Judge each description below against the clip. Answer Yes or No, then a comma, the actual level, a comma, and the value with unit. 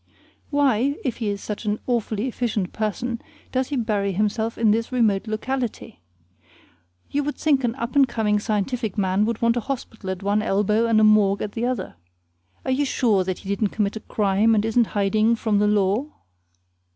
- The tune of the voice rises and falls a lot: No, average, 2.8 semitones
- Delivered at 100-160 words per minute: No, average, 190 wpm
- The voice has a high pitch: Yes, high, 220 Hz